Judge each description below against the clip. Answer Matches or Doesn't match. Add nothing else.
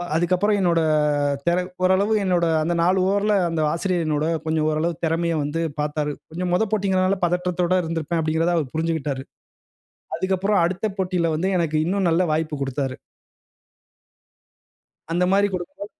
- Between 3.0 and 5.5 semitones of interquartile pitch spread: Doesn't match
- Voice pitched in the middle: Matches